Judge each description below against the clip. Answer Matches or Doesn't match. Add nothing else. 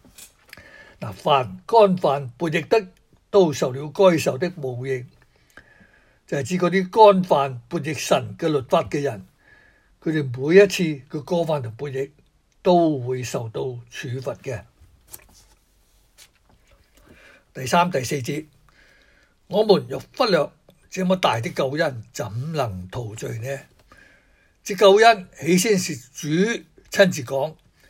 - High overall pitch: Doesn't match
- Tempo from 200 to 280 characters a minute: Doesn't match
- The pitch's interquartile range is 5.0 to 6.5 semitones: Matches